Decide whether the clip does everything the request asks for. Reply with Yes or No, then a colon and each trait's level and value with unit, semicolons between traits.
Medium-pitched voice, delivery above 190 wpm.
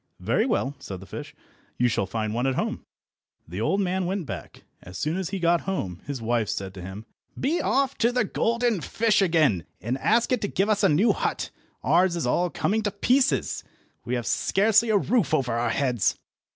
Yes: medium, 170 Hz; fast, 205 wpm